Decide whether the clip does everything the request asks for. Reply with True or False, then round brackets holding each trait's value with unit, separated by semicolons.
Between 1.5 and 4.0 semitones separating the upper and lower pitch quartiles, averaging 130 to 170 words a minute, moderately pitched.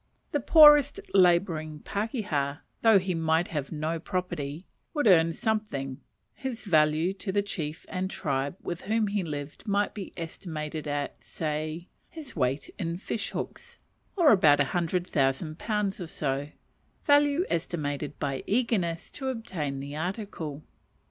False (5.4 semitones; 140 wpm; 170 Hz)